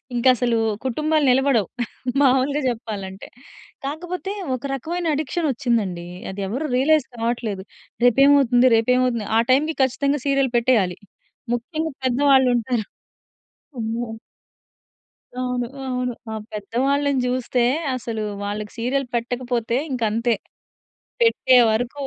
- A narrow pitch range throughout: No, average, 3.2 semitones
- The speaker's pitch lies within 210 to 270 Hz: Yes, very high, 250 Hz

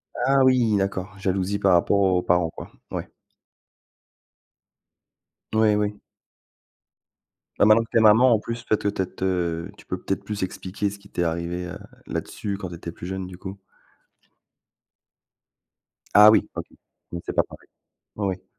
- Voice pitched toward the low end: Yes, low, 100 Hz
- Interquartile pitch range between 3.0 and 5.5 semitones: No, narrow, 2.5 semitones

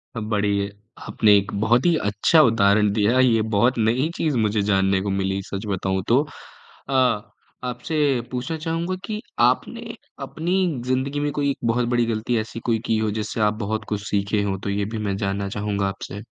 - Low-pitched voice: Yes, low, 110 Hz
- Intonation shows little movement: No, average, 4.2 semitones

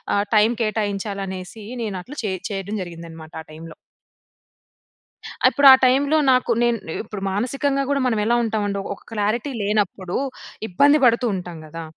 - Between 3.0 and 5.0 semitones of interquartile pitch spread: Yes, average, 4.1 semitones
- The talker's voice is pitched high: Yes, high, 210 Hz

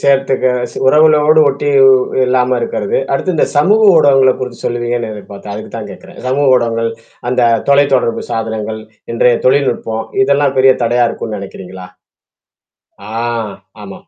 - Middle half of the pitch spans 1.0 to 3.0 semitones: No, average, 3.5 semitones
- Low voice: Yes, low, 125 Hz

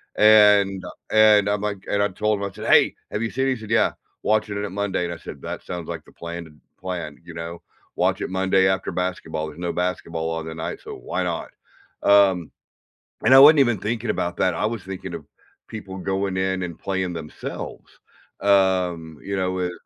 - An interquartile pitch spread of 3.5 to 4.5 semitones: No, average, 3.0 semitones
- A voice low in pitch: Yes, very low, 95 Hz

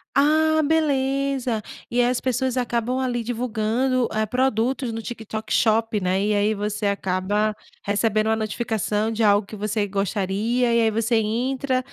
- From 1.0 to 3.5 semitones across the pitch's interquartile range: Yes, average, 3.1 semitones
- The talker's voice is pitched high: Yes, high, 225 Hz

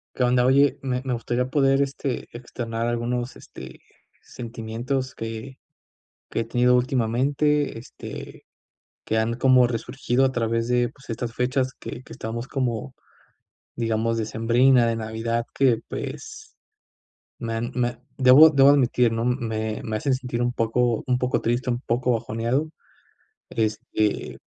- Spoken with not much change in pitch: Yes, narrow, 2.2 semitones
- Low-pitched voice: Yes, low, 120 Hz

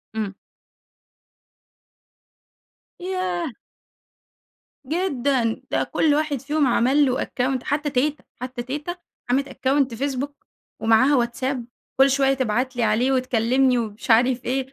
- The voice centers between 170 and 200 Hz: No, very high, 265 Hz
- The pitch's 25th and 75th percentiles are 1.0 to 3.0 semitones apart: Yes, average, 2.7 semitones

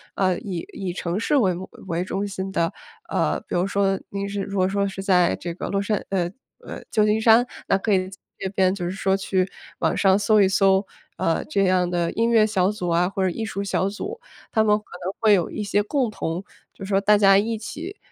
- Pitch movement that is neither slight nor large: No, narrow, 2.0 semitones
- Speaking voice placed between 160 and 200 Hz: Yes, high, 195 Hz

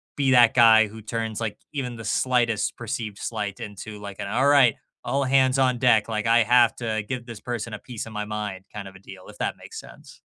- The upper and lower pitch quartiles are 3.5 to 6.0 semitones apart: No, average, 2.7 semitones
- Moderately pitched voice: No, low, 115 Hz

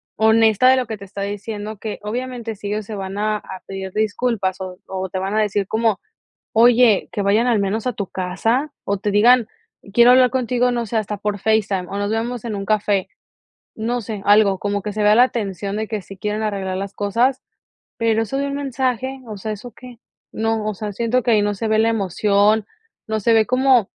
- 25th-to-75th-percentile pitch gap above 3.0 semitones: No, average, 2.7 semitones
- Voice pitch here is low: No, high, 215 Hz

